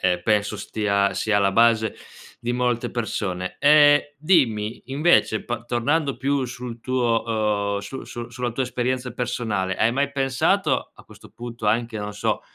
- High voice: No, low, 120 Hz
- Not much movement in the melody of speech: No, average, 3.3 semitones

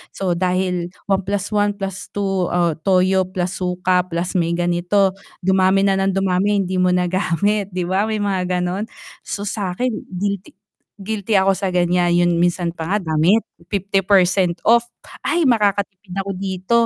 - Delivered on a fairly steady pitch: Yes, narrow, 1.8 semitones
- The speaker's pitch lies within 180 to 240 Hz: Yes, high, 190 Hz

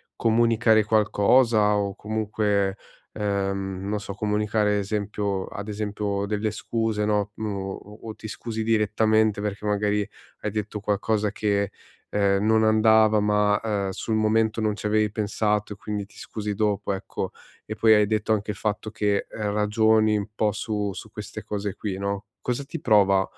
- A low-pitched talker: Yes, low, 105 Hz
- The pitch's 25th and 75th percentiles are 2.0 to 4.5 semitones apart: No, narrow, 1.2 semitones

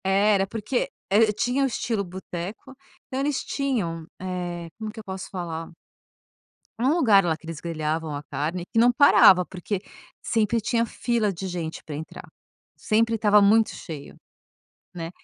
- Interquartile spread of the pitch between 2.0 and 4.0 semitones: No, average, 5.0 semitones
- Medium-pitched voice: No, high, 195 Hz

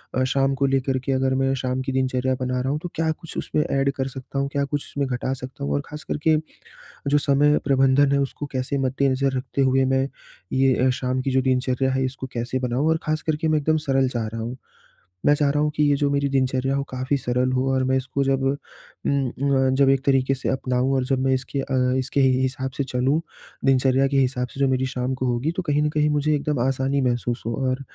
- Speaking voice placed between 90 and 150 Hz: Yes, low, 135 Hz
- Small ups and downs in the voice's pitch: Yes, narrow, 1.4 semitones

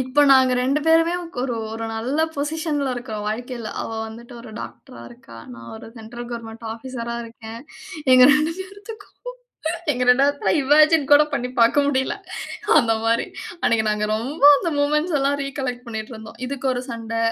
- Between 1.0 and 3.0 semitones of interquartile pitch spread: No, average, 4.0 semitones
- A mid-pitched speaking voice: No, very high, 250 Hz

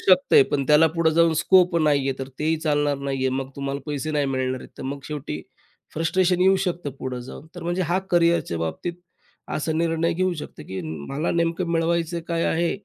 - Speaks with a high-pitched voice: No, medium, 160 Hz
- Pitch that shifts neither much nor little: Yes, average, 3.5 semitones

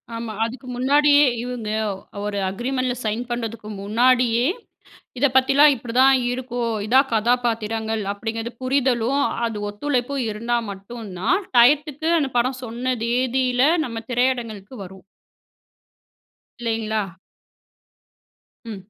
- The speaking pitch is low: No, high, 240 Hz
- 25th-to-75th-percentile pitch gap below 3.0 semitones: Yes, narrow, 2.5 semitones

